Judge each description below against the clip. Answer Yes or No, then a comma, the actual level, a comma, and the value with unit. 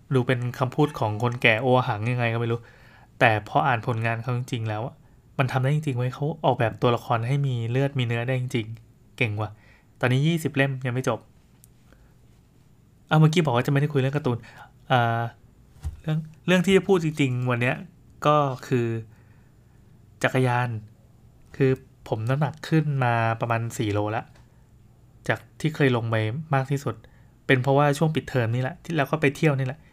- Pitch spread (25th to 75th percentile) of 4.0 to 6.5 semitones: No, average, 2.9 semitones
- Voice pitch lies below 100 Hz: No, low, 125 Hz